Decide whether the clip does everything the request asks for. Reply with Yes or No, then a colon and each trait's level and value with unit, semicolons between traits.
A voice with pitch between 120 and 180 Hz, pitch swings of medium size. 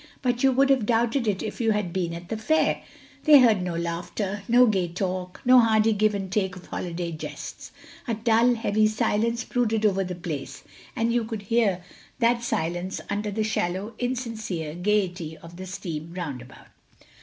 No: high, 210 Hz; average, 4.4 semitones